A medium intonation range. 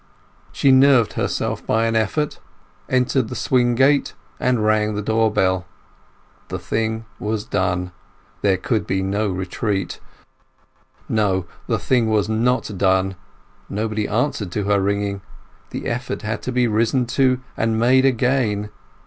Yes: average, 3.5 semitones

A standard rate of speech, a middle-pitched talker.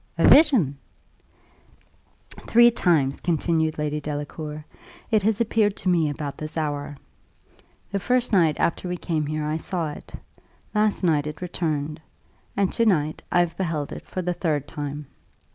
Yes: average, 155 wpm; medium, 160 Hz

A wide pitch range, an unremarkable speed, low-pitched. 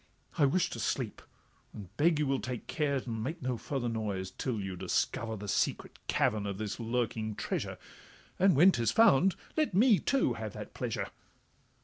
Yes: wide, 6.6 semitones; average, 175 wpm; low, 125 Hz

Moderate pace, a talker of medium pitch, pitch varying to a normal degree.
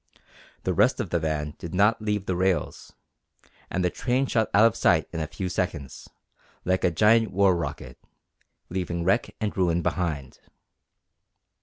No: average, 160 wpm; very low, 90 Hz; average, 3.8 semitones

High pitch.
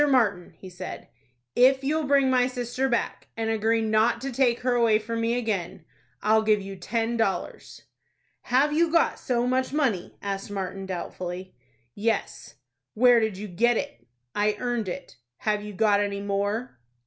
Yes: high, 225 Hz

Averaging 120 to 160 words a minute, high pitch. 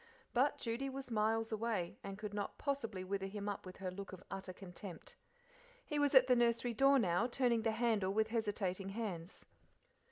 No: average, 185 wpm; high, 220 Hz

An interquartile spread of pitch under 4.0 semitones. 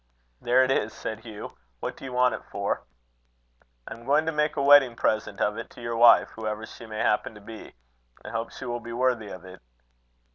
Yes: average, 2.8 semitones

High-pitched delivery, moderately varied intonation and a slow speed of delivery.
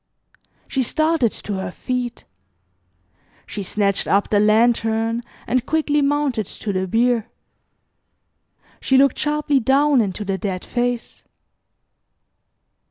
Yes: high, 235 Hz; average, 4.7 semitones; slow, 110 wpm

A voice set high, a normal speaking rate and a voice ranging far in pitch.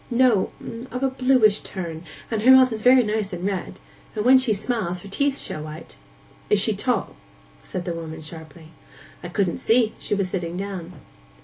Yes: high, 200 Hz; average, 180 wpm; wide, 5.9 semitones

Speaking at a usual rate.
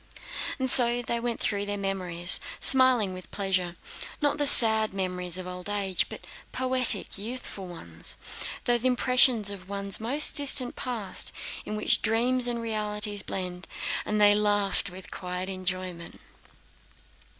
No: slow, 130 wpm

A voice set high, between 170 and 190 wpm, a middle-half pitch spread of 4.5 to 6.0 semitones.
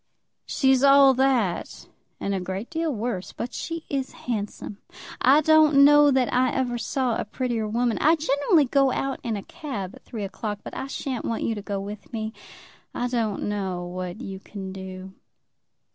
Yes: high, 240 Hz; average, 180 wpm; average, 5.2 semitones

